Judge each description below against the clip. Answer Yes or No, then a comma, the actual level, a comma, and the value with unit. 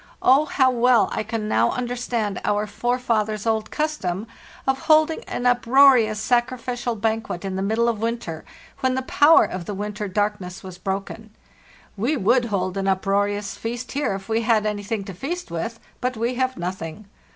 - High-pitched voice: Yes, high, 225 Hz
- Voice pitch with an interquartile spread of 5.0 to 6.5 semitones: No, average, 3.7 semitones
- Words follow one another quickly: No, average, 175 wpm